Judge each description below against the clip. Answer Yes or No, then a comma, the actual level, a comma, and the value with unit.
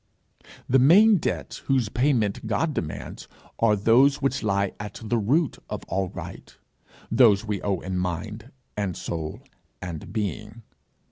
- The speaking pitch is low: Yes, low, 110 Hz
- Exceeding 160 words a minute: No, average, 140 wpm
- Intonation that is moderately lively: Yes, average, 4.8 semitones